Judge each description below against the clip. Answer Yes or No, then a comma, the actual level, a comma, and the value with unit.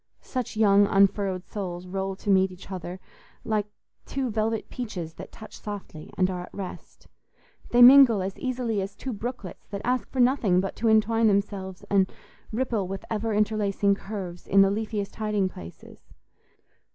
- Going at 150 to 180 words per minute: Yes, average, 165 wpm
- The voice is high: Yes, high, 200 Hz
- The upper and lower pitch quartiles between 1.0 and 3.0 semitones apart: Yes, average, 2.7 semitones